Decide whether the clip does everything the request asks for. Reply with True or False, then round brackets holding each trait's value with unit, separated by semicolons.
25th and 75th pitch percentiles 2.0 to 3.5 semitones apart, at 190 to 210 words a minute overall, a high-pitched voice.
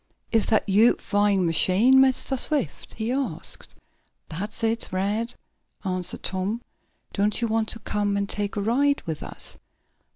False (2.9 semitones; 150 wpm; 210 Hz)